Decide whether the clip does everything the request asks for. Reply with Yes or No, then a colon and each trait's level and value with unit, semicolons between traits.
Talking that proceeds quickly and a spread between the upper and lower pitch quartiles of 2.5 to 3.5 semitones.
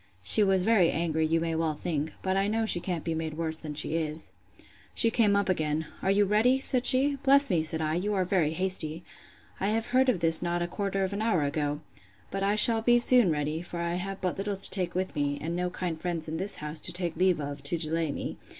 No: fast, 250 wpm; average, 4.1 semitones